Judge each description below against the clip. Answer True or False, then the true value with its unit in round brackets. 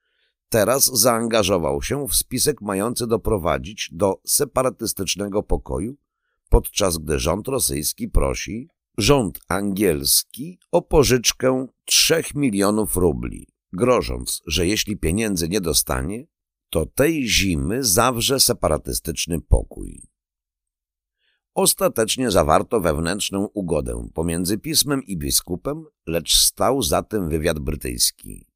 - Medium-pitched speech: False (100 Hz)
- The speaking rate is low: True (100 wpm)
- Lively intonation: True (7.1 semitones)